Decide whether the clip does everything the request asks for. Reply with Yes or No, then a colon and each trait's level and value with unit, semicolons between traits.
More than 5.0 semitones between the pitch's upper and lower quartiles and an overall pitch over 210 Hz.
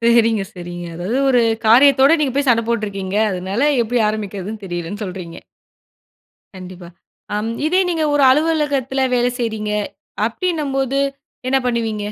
Yes: wide, 5.5 semitones; high, 230 Hz